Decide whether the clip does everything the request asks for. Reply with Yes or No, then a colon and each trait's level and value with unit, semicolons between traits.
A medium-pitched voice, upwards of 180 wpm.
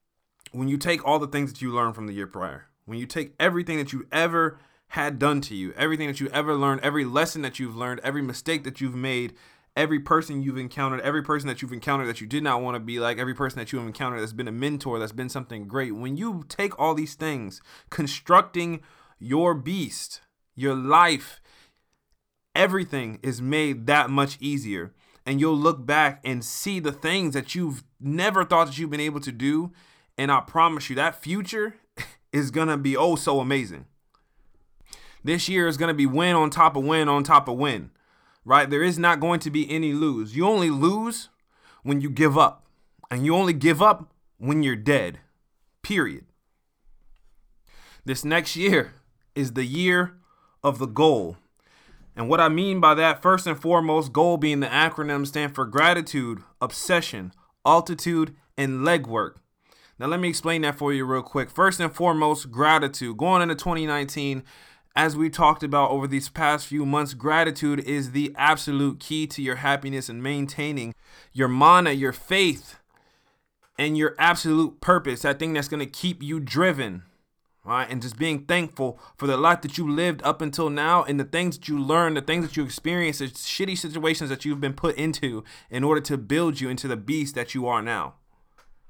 Yes: medium, 145 Hz; average, 190 wpm